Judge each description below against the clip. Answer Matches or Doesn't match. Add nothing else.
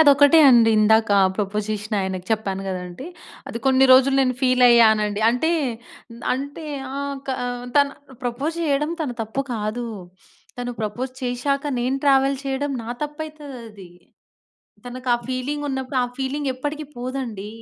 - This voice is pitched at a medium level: Doesn't match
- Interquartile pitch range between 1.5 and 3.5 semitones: Doesn't match